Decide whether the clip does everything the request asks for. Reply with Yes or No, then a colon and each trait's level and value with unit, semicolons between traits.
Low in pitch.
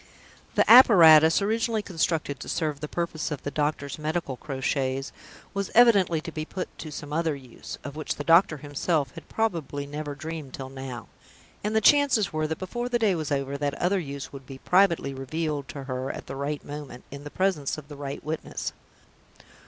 No: medium, 155 Hz